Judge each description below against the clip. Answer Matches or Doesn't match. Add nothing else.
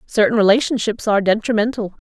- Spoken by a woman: Matches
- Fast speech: Doesn't match